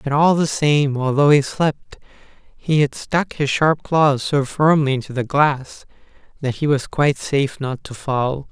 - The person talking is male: Yes, male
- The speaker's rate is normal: Yes, average, 185 wpm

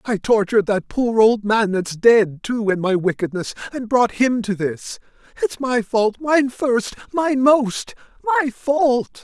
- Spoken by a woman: No, male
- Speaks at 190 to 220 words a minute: No, average, 170 wpm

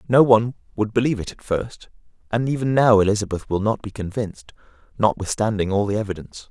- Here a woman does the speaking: No, male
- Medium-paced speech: Yes, average, 175 wpm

